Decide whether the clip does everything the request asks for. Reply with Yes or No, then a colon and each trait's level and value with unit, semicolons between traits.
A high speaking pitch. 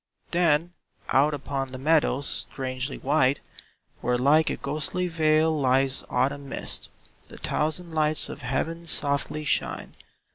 No: medium, 145 Hz